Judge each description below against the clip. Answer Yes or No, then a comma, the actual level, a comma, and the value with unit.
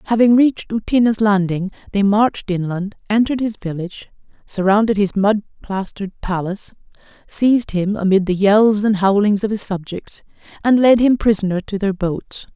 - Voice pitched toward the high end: Yes, high, 205 Hz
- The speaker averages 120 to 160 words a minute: Yes, average, 155 wpm